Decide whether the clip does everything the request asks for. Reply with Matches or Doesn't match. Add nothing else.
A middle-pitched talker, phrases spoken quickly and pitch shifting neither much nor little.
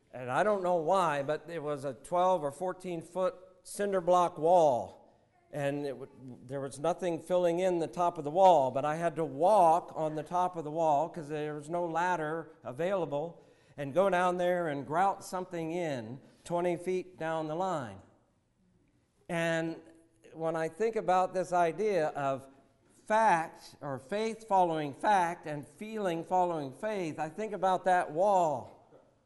Doesn't match